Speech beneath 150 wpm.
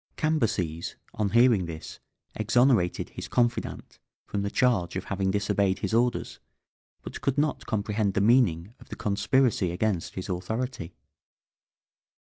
Yes: slow, 135 wpm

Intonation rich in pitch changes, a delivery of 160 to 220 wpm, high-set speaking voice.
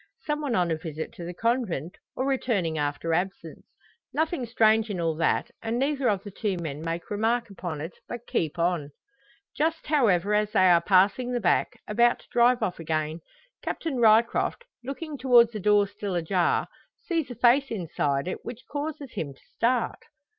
Yes: wide, 6.2 semitones; average, 180 wpm; high, 210 Hz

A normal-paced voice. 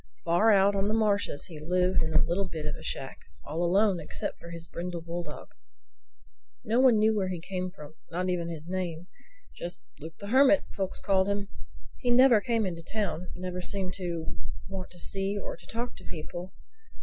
Yes: average, 185 wpm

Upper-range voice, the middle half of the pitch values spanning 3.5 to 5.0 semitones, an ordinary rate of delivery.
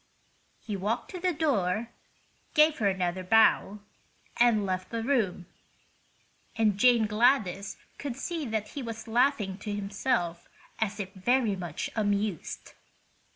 No: high, 215 Hz; average, 3.9 semitones; slow, 130 wpm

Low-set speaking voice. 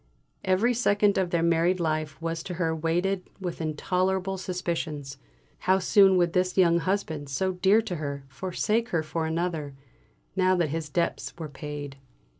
No: medium, 175 Hz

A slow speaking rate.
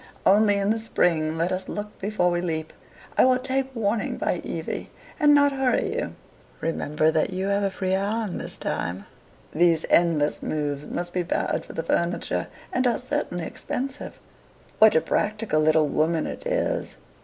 No: average, 170 wpm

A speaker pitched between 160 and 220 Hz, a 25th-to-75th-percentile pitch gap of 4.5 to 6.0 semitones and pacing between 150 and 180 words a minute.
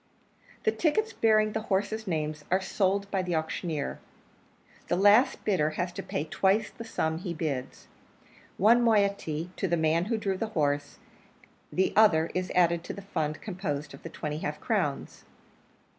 Yes: medium, 185 Hz; average, 4.9 semitones; average, 165 wpm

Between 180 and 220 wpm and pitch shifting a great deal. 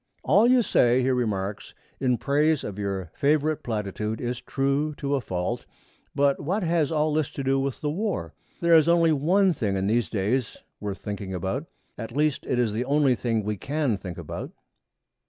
Yes: average, 190 wpm; wide, 6.2 semitones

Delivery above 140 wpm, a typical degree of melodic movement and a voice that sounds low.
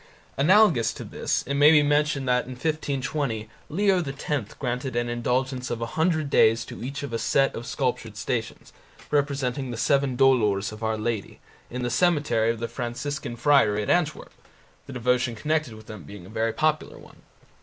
Yes: average, 180 wpm; average, 4.0 semitones; low, 125 Hz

